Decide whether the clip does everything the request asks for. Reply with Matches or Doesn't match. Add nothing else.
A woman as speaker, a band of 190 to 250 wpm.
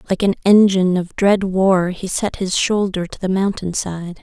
Matches